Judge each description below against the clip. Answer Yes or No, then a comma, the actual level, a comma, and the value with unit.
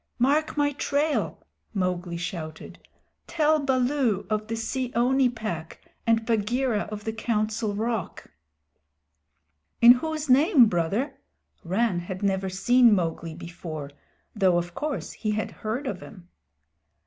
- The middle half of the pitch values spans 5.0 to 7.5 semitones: Yes, wide, 5.6 semitones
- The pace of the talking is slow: Yes, slow, 125 wpm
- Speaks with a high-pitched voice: Yes, high, 220 Hz